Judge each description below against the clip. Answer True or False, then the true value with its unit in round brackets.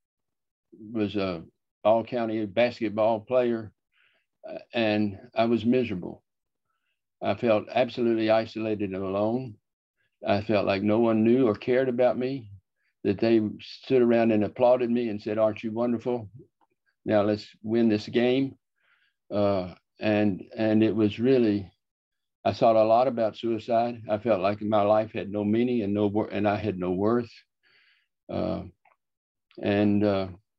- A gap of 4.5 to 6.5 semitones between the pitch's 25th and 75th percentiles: False (2.4 semitones)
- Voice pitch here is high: False (110 Hz)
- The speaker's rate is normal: True (145 wpm)